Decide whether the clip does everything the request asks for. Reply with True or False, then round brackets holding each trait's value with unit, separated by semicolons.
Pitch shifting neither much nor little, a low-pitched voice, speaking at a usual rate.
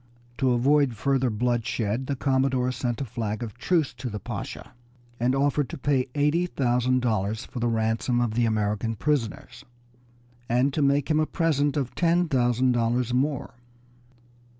True (3.2 semitones; 125 Hz; 160 wpm)